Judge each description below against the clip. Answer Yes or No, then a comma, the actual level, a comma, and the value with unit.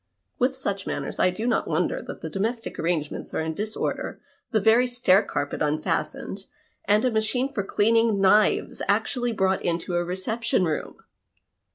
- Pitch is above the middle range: Yes, high, 205 Hz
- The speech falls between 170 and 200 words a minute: No, average, 160 wpm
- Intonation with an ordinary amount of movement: Yes, average, 4.1 semitones